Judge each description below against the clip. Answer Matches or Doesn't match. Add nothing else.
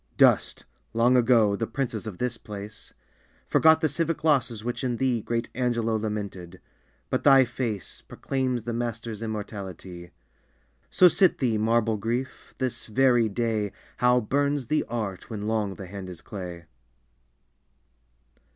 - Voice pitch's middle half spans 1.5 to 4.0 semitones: Matches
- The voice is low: Matches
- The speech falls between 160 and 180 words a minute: Doesn't match